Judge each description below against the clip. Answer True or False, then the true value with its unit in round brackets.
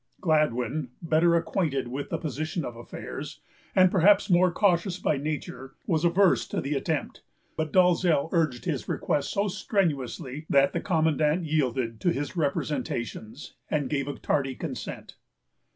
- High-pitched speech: False (155 Hz)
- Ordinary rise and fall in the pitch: True (4.0 semitones)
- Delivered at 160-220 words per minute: False (145 wpm)